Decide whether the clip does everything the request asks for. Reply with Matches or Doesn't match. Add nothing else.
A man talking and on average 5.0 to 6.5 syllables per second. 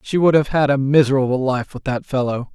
Matches